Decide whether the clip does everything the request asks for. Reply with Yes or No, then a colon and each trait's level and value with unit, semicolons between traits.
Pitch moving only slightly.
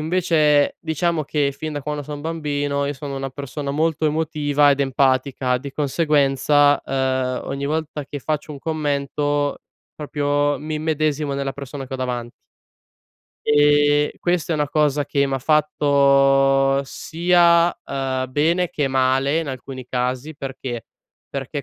Yes: narrow, 1.9 semitones